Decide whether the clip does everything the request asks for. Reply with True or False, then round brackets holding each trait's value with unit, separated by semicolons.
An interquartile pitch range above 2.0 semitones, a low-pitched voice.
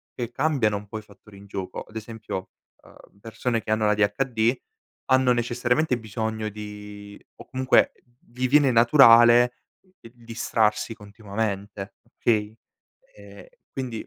True (2.7 semitones; 110 Hz)